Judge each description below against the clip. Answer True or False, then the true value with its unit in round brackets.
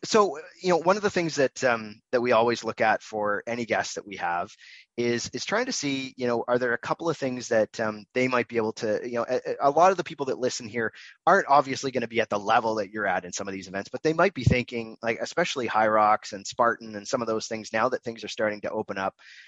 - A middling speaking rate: False (285 wpm)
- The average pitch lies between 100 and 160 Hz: True (120 Hz)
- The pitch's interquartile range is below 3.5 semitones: False (4.0 semitones)